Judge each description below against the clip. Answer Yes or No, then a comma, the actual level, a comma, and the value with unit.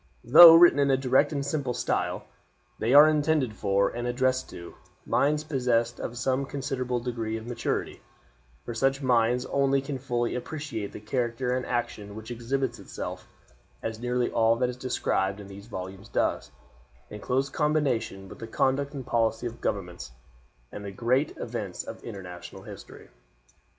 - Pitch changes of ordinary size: Yes, average, 3.2 semitones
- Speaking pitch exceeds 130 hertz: No, low, 125 Hz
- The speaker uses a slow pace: No, average, 160 wpm